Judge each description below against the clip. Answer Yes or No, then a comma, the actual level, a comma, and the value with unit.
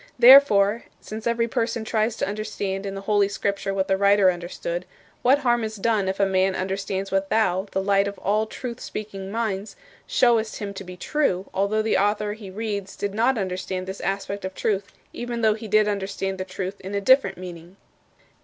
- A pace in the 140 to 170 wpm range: No, average, 200 wpm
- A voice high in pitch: Yes, high, 200 Hz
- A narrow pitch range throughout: Yes, narrow, 2.3 semitones